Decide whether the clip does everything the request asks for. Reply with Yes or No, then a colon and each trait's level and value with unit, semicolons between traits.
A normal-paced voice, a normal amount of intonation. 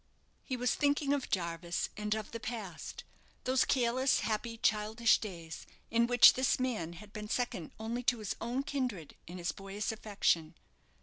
Yes: average, 165 wpm; average, 4.1 semitones